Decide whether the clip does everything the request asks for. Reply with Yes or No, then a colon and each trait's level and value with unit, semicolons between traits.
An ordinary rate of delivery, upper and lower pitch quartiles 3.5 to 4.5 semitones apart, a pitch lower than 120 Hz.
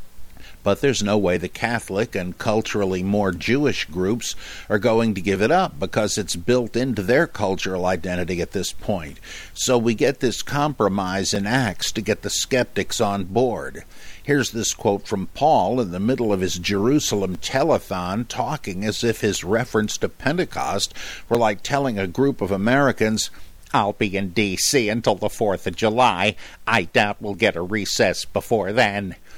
Yes: average, 170 wpm; average, 3.8 semitones; low, 105 Hz